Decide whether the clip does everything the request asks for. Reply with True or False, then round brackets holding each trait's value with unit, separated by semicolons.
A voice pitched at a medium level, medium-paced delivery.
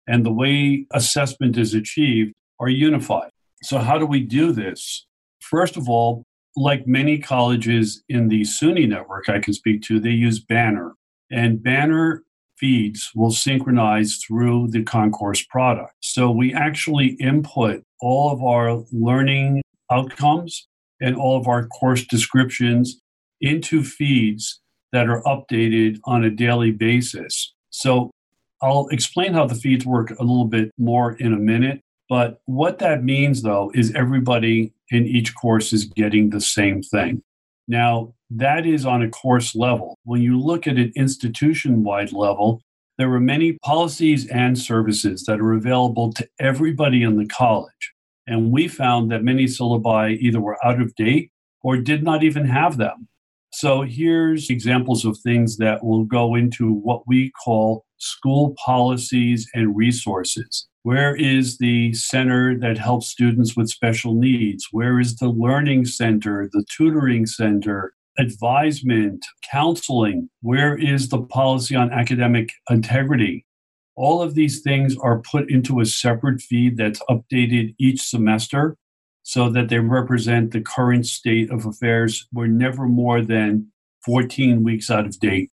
False (120 Hz; 150 wpm)